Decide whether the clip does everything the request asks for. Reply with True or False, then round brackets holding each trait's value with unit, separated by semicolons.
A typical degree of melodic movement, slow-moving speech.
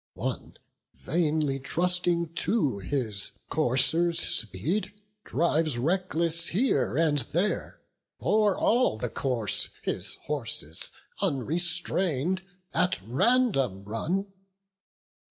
False (6.0 semitones; 85 wpm)